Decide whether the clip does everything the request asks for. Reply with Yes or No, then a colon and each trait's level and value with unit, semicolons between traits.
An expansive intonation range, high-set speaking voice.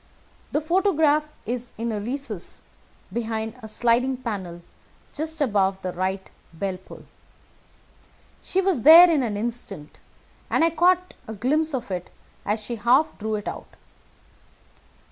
Yes: wide, 6.7 semitones; high, 235 Hz